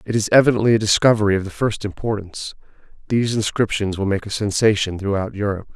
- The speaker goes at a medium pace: Yes, average, 175 wpm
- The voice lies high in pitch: No, low, 105 Hz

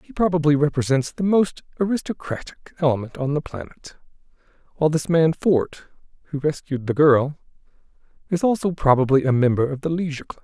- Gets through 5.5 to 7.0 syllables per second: Yes, 5.9 syllables/s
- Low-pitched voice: No, medium, 150 Hz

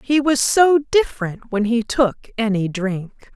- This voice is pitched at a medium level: No, high, 240 Hz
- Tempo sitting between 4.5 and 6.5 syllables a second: No, 4.0 syllables/s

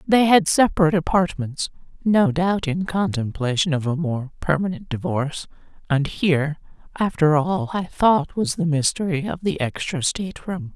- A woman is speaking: Yes, female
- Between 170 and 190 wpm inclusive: No, average, 145 wpm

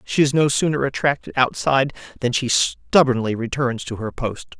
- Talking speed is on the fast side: No, average, 170 wpm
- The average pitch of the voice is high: No, low, 130 Hz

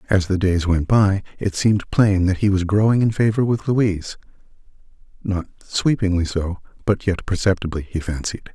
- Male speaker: Yes, male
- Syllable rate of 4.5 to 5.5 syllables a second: Yes, 5.2 syllables/s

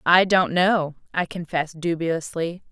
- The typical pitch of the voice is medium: Yes, medium, 170 Hz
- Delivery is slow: Yes, slow, 130 wpm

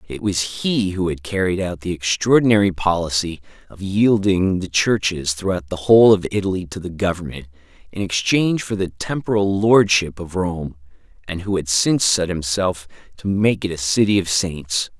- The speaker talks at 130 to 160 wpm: No, average, 170 wpm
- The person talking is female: No, male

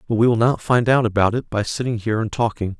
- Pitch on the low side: Yes, low, 115 Hz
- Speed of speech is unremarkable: No, fast, 280 wpm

